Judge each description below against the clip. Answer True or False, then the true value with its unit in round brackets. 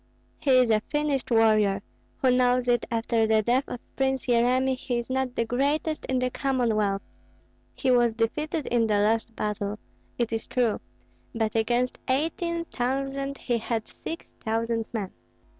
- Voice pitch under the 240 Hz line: False (245 Hz)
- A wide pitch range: False (2.8 semitones)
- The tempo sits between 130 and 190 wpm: True (160 wpm)